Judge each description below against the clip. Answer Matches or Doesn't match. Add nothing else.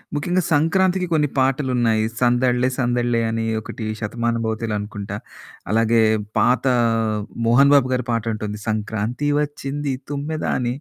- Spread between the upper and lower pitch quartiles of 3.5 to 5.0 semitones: Matches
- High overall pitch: Doesn't match